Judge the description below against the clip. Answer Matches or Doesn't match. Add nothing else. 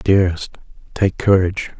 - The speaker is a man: Matches